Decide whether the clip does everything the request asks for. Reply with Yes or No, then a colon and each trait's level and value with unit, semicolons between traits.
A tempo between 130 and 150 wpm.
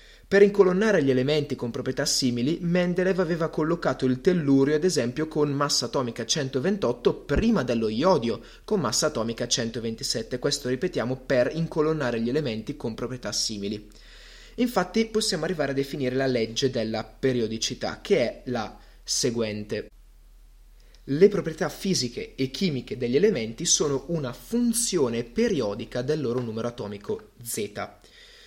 Yes: average, 135 wpm